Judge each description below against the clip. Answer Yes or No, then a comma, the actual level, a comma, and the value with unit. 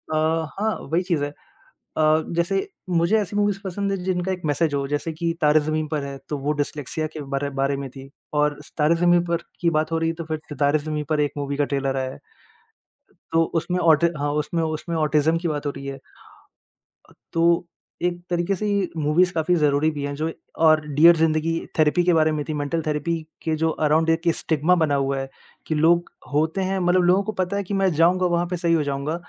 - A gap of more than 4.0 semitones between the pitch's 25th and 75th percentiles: No, average, 2.7 semitones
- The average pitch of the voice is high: No, medium, 160 Hz